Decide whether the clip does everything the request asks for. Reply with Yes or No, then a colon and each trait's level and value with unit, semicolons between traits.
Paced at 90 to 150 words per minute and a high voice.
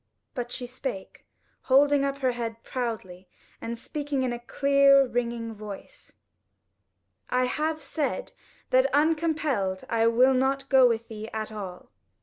Yes: average, 140 wpm; very high, 250 Hz